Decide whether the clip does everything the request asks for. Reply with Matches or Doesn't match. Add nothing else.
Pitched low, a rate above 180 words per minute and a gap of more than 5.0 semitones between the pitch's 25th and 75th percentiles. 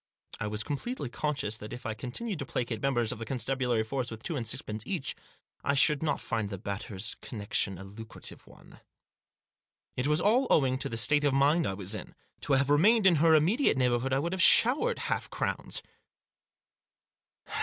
Matches